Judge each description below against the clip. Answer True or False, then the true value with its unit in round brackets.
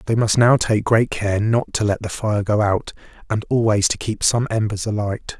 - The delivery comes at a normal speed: False (220 wpm)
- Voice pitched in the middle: False (105 Hz)